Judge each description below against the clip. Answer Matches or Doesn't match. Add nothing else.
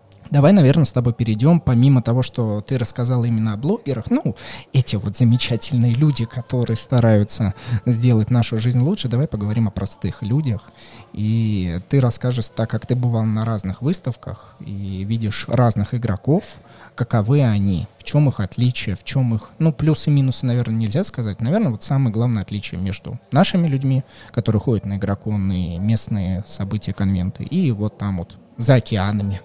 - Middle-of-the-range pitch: Doesn't match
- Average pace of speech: Doesn't match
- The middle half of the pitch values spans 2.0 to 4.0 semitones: Matches